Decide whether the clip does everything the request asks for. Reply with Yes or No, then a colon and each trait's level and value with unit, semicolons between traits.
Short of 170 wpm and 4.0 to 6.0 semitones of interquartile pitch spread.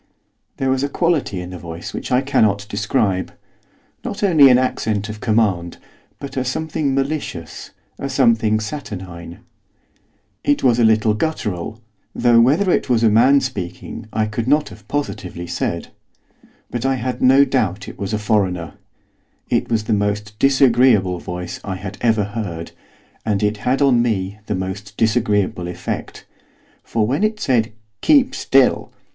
Yes: average, 155 wpm; average, 4.7 semitones